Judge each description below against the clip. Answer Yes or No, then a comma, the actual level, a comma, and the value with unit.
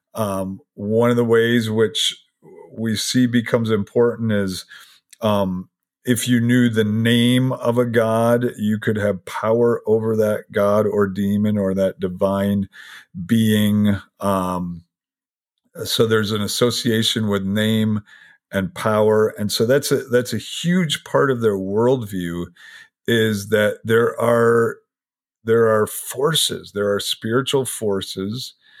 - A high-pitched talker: No, low, 110 Hz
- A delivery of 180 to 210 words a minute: No, slow, 135 wpm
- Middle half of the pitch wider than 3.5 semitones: No, average, 2.7 semitones